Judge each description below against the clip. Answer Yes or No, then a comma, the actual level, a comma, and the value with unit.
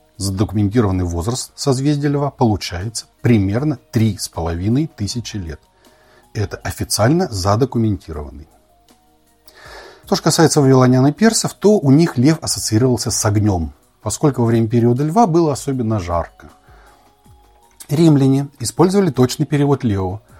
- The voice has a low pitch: Yes, low, 120 Hz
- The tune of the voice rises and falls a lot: Yes, wide, 6.0 semitones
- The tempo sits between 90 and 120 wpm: Yes, slow, 110 wpm